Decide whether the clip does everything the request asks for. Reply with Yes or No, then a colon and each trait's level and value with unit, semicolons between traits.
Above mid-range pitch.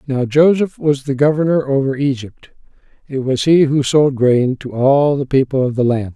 No: medium, 140 Hz